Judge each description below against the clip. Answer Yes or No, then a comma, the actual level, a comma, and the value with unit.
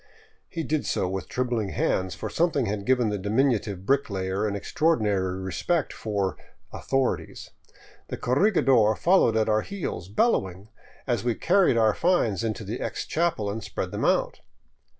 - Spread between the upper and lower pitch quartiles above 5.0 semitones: Yes, wide, 5.5 semitones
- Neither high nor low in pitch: No, low, 110 Hz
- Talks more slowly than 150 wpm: No, average, 160 wpm